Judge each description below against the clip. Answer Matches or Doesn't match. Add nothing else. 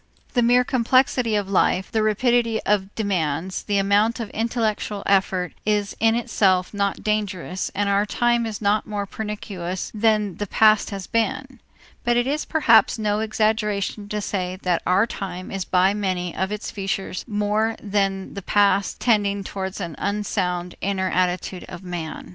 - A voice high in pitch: Matches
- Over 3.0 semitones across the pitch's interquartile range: Doesn't match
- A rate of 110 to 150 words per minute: Doesn't match